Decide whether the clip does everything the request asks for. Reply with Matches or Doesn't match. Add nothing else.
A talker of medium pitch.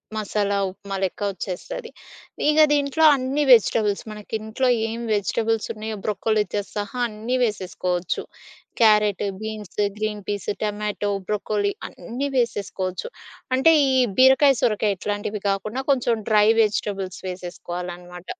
Doesn't match